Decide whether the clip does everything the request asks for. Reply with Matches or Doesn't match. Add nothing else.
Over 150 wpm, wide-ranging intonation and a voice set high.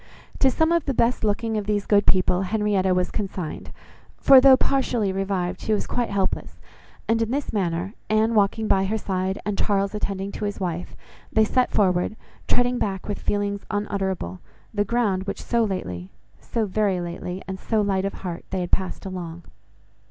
Doesn't match